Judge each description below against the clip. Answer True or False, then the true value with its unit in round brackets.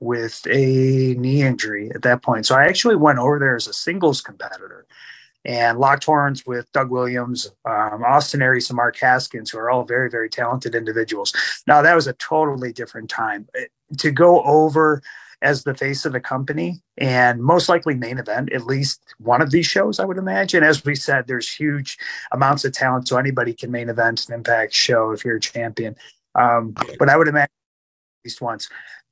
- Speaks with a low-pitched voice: True (130 Hz)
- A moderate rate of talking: True (195 wpm)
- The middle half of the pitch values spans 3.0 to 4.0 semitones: True (3.6 semitones)